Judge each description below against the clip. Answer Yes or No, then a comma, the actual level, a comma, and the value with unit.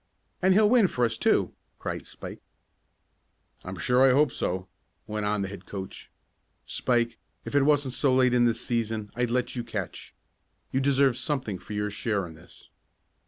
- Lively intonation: No, average, 4.4 semitones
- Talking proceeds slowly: No, average, 175 wpm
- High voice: No, low, 120 Hz